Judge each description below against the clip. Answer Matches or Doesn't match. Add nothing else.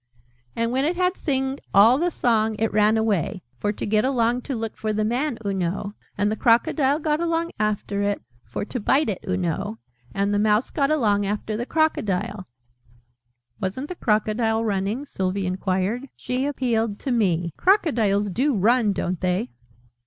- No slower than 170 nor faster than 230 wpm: Matches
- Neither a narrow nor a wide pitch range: Matches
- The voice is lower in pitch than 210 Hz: Doesn't match